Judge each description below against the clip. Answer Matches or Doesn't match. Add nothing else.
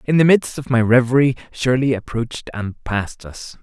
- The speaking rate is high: Doesn't match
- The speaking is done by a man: Matches